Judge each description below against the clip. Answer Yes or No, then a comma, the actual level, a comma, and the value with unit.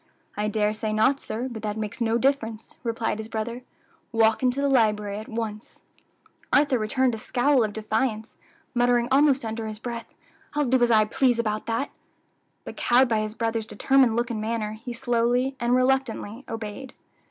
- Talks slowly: No, average, 175 wpm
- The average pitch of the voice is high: Yes, high, 230 Hz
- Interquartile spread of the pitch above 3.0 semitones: No, narrow, 2.6 semitones